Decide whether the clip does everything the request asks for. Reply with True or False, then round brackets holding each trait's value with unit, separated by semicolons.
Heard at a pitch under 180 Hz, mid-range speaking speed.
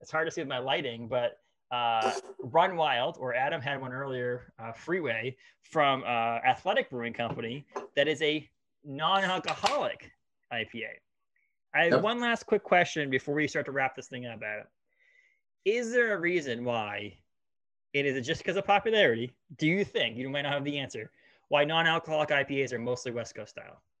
True (140 Hz; 185 wpm)